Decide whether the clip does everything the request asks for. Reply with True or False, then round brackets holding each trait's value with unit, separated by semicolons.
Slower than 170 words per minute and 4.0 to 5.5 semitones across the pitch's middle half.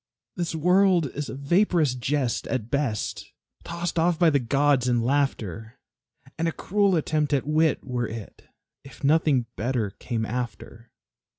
True (150 wpm; 5.0 semitones)